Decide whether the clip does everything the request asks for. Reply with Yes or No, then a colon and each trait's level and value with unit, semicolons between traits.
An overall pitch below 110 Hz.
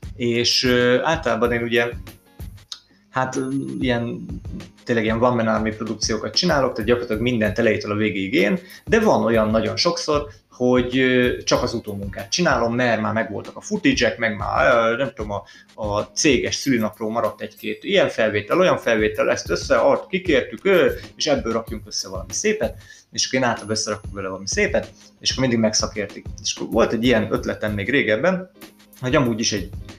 No: low, 115 Hz